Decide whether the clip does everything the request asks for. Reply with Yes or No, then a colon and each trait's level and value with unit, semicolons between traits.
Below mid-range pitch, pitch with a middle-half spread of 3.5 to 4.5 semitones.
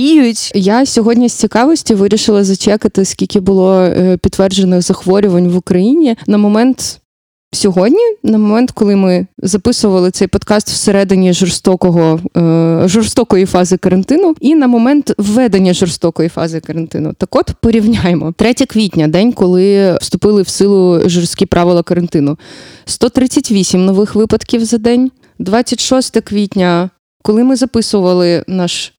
No: high, 200 Hz; average, 4.0 semitones